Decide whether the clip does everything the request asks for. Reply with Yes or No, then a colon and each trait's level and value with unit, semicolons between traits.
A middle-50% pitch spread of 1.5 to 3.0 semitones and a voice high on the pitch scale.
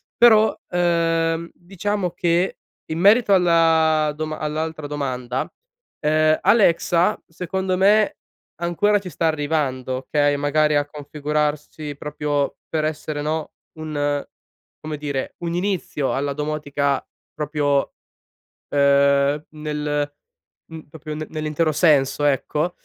No: narrow, 2.6 semitones; medium, 155 Hz